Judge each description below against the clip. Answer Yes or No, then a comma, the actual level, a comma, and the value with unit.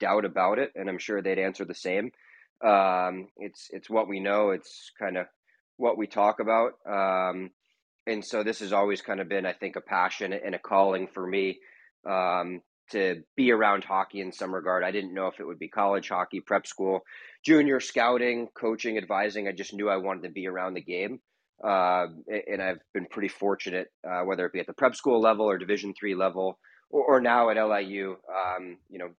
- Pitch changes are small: Yes, narrow, 1.9 semitones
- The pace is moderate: No, fast, 210 wpm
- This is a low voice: Yes, very low, 95 Hz